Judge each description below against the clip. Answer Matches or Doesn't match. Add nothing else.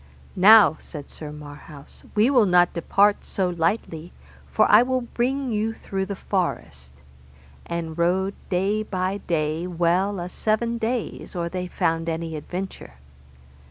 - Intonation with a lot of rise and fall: Doesn't match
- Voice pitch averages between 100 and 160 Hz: Doesn't match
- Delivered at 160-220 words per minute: Doesn't match